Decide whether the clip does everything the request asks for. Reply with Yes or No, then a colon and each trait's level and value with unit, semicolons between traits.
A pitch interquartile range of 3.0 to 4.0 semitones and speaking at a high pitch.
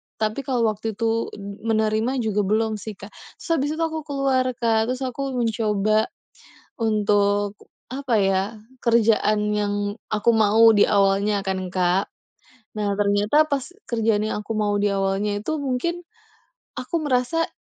Yes: average, 3.4 semitones; high, 220 Hz